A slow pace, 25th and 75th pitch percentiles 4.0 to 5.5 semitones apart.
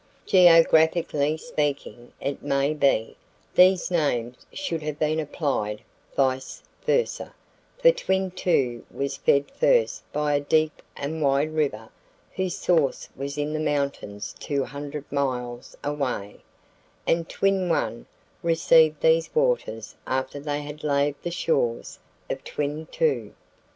No: slow, 125 wpm; average, 3.2 semitones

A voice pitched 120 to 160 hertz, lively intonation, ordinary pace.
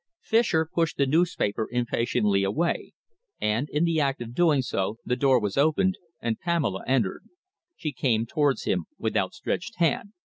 Yes: low, 135 Hz; wide, 6.6 semitones; average, 155 wpm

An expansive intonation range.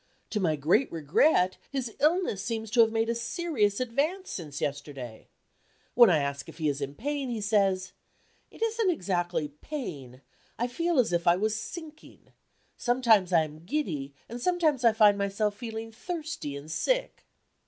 Yes: wide, 8.2 semitones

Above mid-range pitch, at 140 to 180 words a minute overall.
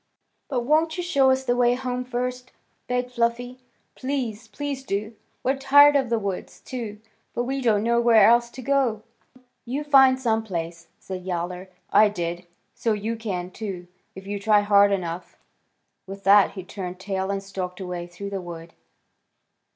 Yes: high, 220 Hz; average, 175 wpm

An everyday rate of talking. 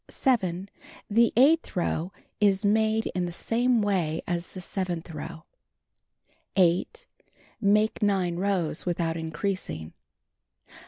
No: slow, 110 wpm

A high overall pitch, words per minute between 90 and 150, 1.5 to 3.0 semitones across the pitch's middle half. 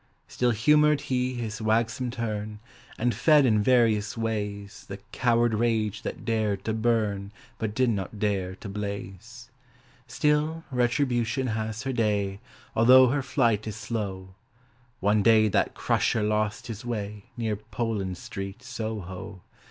No: low, 110 Hz; slow, 135 wpm; average, 2.7 semitones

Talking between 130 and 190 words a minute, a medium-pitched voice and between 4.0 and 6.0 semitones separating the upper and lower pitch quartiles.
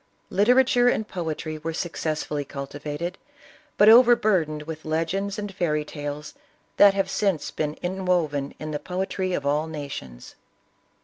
Yes: slow, 135 wpm; medium, 160 Hz; average, 4.4 semitones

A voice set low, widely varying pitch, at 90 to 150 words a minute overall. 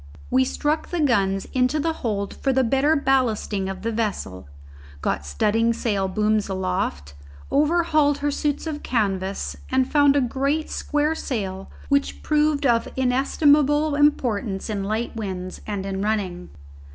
No: high, 235 Hz; wide, 6.6 semitones; average, 145 wpm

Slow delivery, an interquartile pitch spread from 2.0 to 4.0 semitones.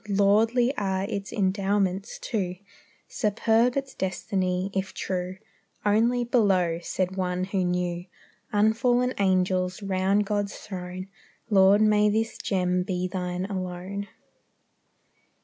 Yes: slow, 110 wpm; narrow, 2.4 semitones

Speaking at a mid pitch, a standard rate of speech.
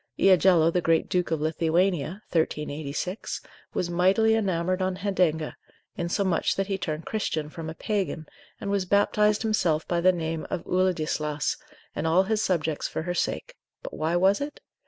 Yes: medium, 175 Hz; average, 160 wpm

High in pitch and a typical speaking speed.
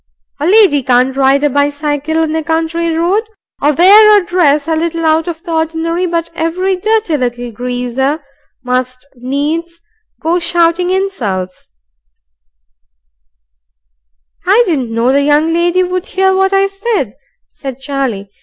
Yes: very high, 315 Hz; average, 145 wpm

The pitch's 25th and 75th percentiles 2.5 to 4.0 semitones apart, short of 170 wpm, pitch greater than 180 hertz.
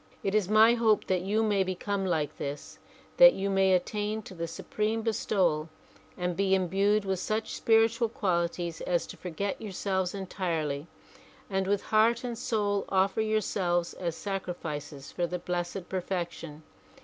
Yes: average, 3.3 semitones; average, 150 wpm; high, 190 Hz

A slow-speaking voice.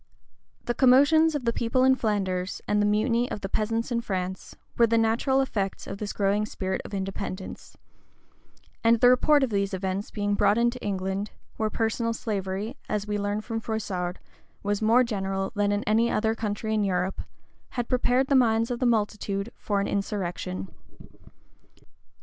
No: average, 165 wpm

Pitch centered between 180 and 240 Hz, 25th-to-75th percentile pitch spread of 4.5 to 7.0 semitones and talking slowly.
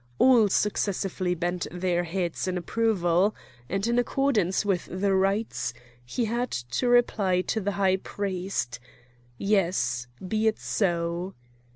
No: high, 190 Hz; average, 3.4 semitones; slow, 130 wpm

